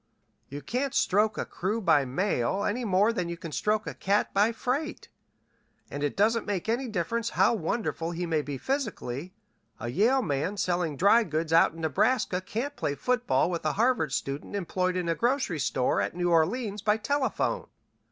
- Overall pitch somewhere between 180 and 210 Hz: Yes, high, 190 Hz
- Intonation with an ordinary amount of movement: No, wide, 5.9 semitones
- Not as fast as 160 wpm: No, average, 180 wpm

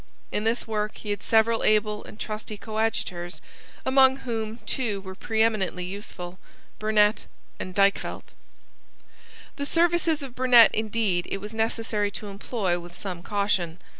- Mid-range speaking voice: No, high, 215 Hz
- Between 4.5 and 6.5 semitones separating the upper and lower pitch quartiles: No, narrow, 2.4 semitones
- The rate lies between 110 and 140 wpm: Yes, slow, 135 wpm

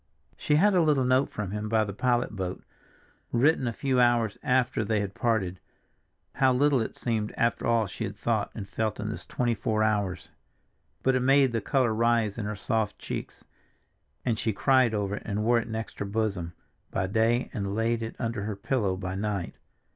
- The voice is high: No, low, 110 Hz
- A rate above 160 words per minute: Yes, average, 200 wpm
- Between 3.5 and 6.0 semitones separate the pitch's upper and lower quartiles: No, average, 3.1 semitones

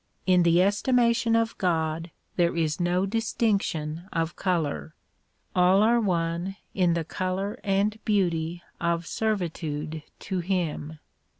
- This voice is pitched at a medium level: Yes, medium, 180 Hz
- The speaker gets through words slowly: Yes, slow, 120 wpm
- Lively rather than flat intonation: No, average, 3.3 semitones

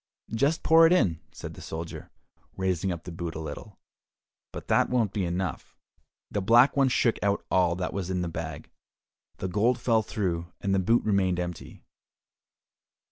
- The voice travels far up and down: No, average, 4.6 semitones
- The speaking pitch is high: No, very low, 95 Hz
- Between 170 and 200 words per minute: Yes, average, 175 wpm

